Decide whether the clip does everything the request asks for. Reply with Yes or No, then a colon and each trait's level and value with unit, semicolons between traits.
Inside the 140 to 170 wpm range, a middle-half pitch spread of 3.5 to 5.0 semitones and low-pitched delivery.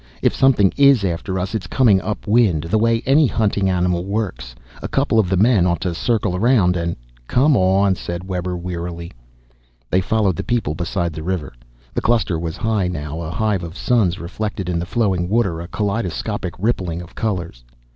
No: average, 190 wpm; average, 4.1 semitones; very low, 95 Hz